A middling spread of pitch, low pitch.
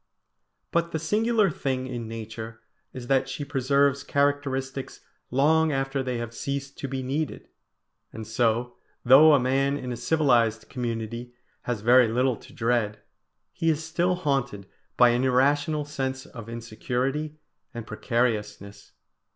Yes: average, 3.3 semitones; low, 130 Hz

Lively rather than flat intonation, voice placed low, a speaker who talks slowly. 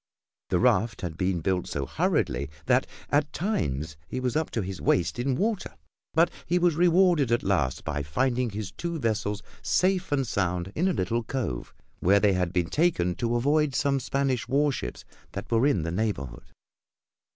No: wide, 8.1 semitones; low, 115 Hz; average, 175 wpm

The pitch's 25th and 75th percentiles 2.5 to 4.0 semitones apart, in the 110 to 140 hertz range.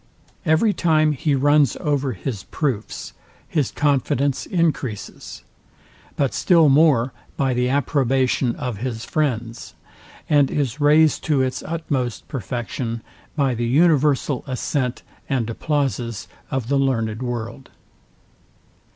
Yes: average, 3.4 semitones; low, 135 Hz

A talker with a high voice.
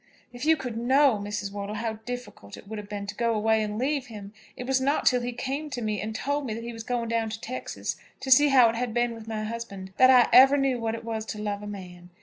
Yes: high, 230 Hz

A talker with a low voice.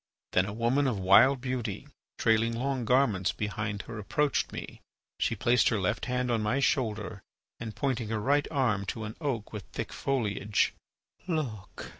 Yes: low, 115 Hz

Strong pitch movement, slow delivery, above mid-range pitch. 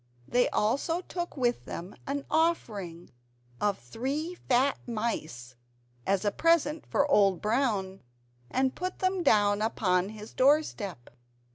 Yes: wide, 6.5 semitones; slow, 130 wpm; high, 235 Hz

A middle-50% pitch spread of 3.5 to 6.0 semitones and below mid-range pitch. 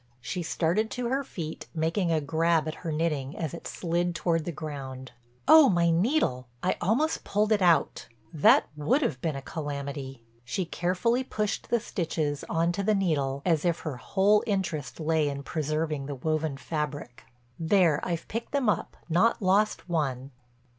No: average, 4.6 semitones; medium, 165 Hz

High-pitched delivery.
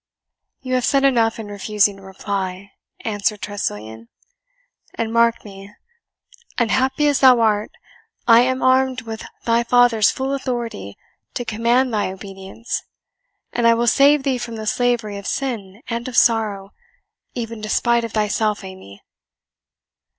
Yes: high, 225 Hz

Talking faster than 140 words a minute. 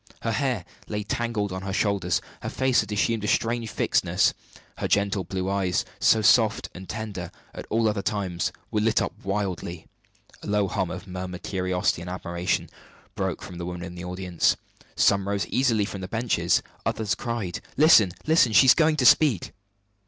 Yes: average, 180 wpm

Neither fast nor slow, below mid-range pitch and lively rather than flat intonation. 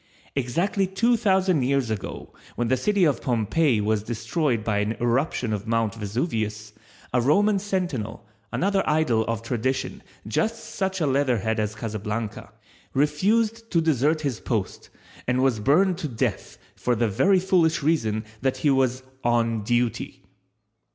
Yes: average, 145 wpm; low, 130 Hz; wide, 6.9 semitones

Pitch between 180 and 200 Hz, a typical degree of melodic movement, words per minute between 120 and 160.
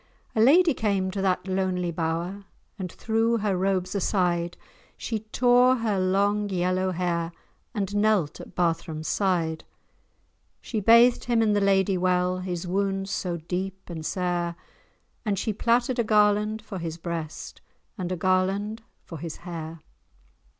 Yes: high, 190 Hz; average, 3.1 semitones; average, 145 wpm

